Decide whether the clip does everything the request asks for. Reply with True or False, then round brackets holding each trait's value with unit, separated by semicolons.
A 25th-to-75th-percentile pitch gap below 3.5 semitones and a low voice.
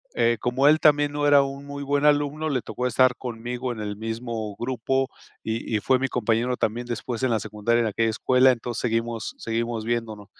True (2.8 semitones; 120 Hz)